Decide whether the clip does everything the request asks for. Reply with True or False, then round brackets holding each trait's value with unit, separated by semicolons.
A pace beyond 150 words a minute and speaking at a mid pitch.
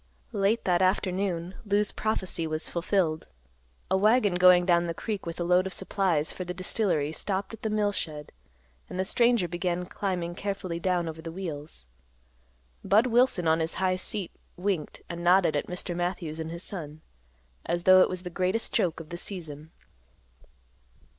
True (175 wpm; 180 Hz)